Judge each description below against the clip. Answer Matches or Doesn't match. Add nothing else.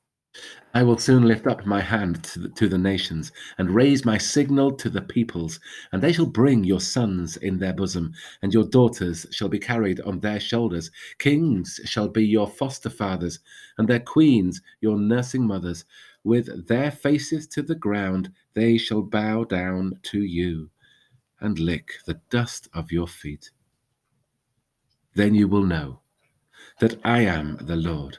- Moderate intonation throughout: Matches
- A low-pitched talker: Matches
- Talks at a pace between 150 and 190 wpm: Matches